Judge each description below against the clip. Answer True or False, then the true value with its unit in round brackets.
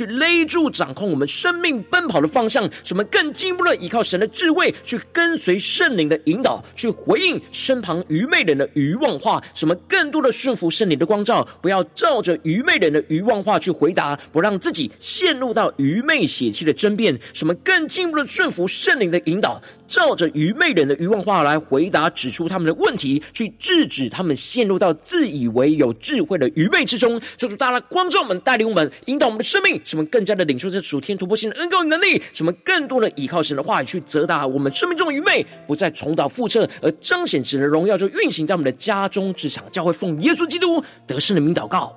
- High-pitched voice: True (205 Hz)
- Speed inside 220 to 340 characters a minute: True (335 characters per minute)